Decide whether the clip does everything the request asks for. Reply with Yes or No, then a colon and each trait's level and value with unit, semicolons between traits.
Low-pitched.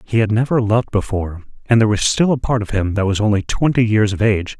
Yes: low, 110 Hz